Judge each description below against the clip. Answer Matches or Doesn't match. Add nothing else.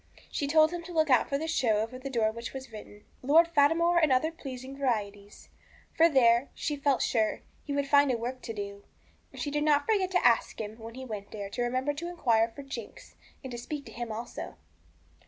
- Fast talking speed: Matches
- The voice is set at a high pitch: Matches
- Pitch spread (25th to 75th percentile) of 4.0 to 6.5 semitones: Matches